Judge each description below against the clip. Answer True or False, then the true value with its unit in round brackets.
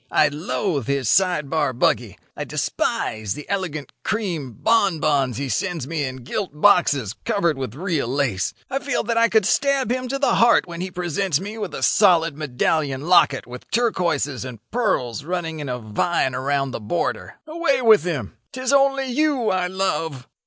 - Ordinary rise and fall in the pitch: False (7.4 semitones)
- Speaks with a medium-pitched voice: True (165 Hz)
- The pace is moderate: True (175 wpm)